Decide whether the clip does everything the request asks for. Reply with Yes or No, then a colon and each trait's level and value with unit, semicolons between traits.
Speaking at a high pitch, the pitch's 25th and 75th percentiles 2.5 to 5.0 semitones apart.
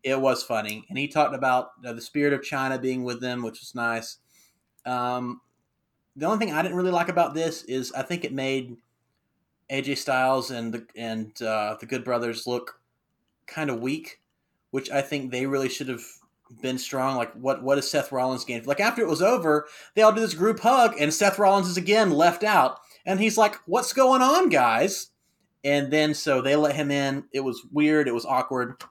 No: low, 135 Hz; average, 4.7 semitones